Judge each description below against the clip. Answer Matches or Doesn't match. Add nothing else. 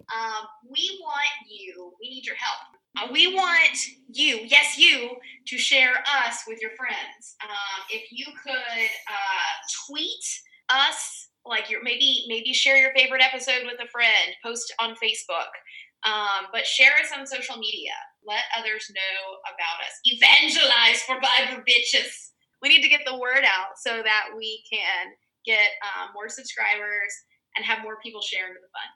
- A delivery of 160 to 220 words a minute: Matches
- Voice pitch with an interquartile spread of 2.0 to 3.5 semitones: Doesn't match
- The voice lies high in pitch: Matches